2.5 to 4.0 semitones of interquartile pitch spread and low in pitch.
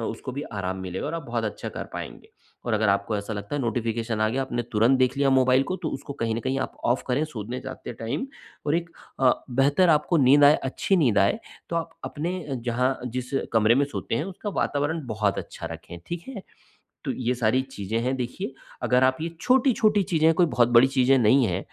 No: average, 4.5 semitones; low, 130 Hz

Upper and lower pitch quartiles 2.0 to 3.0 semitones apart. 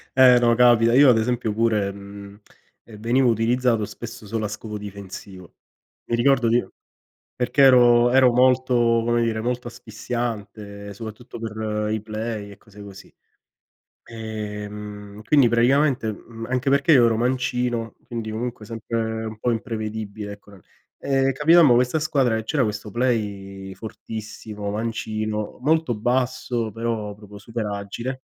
Yes: average, 2.7 semitones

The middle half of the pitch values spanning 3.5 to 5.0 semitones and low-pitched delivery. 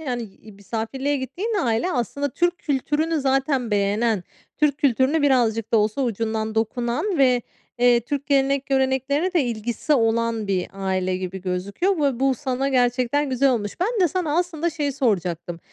No: average, 4.4 semitones; very high, 255 Hz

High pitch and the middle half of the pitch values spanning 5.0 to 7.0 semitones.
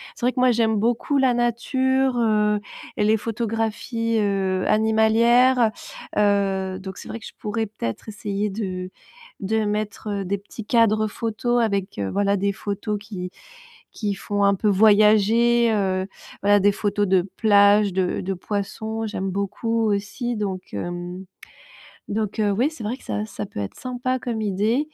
No: high, 210 Hz; narrow, 2.4 semitones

